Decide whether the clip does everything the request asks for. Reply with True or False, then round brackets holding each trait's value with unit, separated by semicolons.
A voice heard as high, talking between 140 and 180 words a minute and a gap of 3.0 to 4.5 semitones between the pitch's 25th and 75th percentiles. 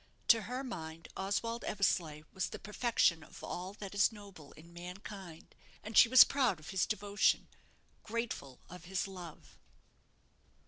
True (195 Hz; 145 wpm; 4.0 semitones)